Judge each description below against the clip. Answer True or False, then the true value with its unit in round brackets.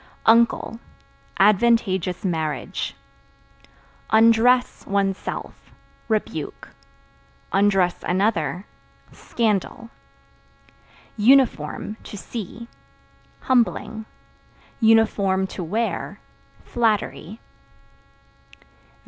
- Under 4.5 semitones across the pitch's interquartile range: True (3.2 semitones)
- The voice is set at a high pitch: True (215 Hz)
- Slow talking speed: True (50 wpm)